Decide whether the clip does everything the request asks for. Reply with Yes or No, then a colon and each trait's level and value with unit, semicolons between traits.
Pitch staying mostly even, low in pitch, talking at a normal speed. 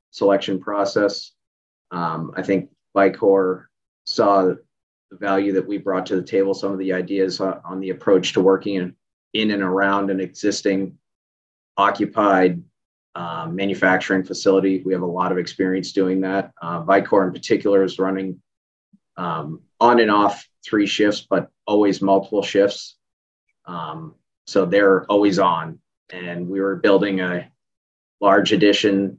Yes: narrow, 1.2 semitones; very low, 95 Hz; average, 145 wpm